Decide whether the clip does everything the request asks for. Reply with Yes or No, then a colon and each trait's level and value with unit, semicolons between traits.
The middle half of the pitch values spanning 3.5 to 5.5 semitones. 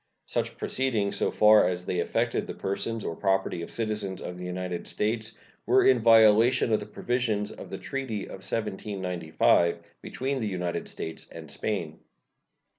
Yes: average, 3.8 semitones